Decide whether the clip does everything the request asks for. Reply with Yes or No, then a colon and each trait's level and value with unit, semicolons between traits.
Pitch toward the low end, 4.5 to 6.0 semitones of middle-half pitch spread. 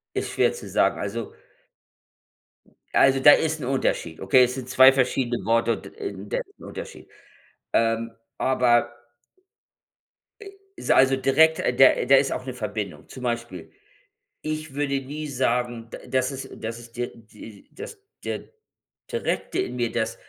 No: low, 125 Hz; narrow, 2.6 semitones